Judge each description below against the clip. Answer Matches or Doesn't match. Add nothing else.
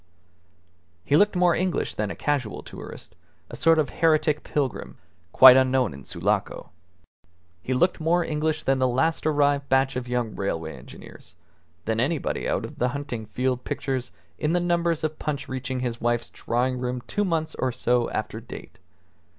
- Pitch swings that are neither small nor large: Matches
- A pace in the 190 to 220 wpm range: Doesn't match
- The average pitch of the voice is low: Matches